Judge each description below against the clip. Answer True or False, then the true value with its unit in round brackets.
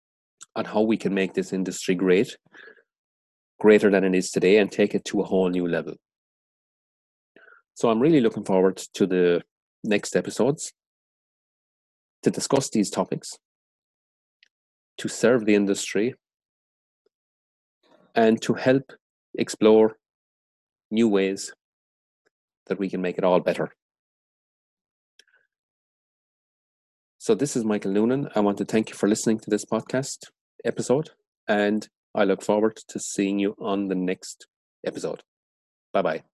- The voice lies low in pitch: True (100 Hz)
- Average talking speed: False (130 wpm)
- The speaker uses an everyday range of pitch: True (4.0 semitones)